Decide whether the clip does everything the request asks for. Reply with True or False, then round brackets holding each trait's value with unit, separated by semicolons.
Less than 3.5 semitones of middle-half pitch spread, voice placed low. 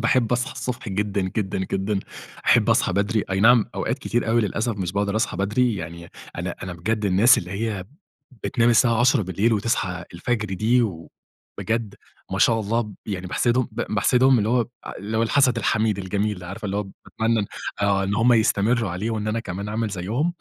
True (3.1 semitones; 110 Hz)